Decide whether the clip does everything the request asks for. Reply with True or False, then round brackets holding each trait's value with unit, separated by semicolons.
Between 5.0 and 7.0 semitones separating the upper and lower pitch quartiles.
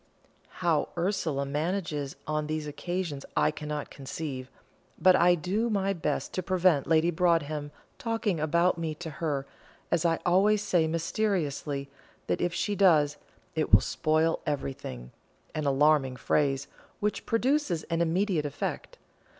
False (3.7 semitones)